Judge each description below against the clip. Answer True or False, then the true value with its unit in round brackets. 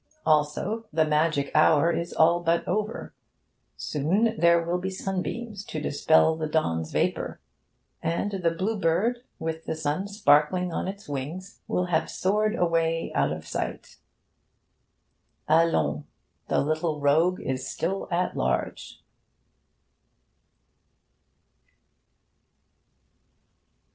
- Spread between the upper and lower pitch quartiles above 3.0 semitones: True (3.4 semitones)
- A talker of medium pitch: True (165 Hz)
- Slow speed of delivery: True (110 wpm)